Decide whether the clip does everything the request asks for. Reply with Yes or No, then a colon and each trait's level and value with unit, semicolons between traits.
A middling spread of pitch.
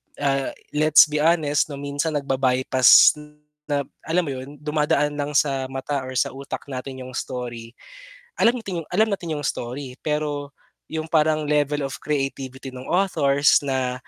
No: narrow, 2.3 semitones